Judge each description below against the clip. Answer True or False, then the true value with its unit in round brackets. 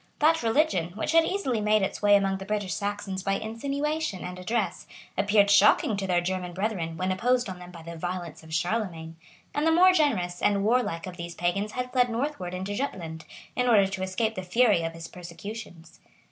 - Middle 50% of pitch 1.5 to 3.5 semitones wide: False (4.5 semitones)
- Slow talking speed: False (200 wpm)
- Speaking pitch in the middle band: False (195 Hz)